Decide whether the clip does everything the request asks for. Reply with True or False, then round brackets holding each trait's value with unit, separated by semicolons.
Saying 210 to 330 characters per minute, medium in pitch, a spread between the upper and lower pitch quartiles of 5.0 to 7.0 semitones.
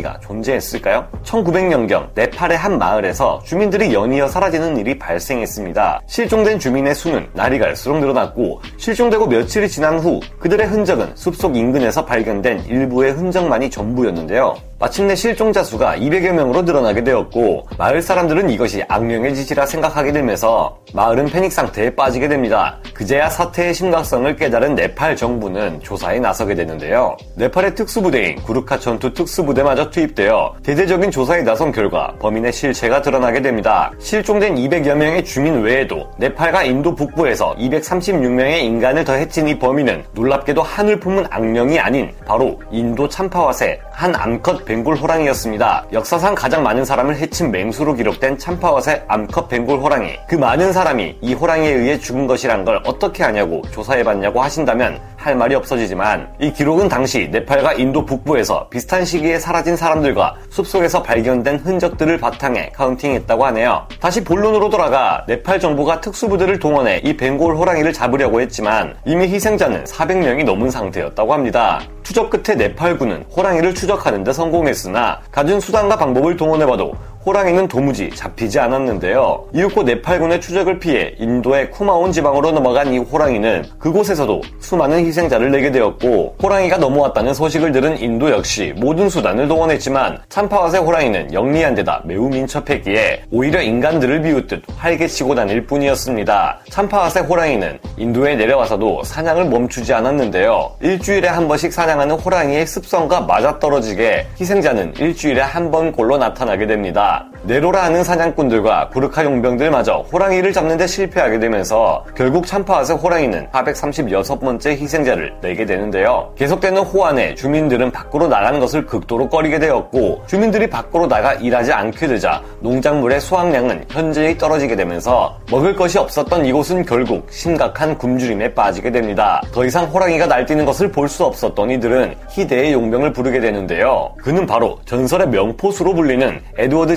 False (390 characters per minute; 155 Hz; 5.8 semitones)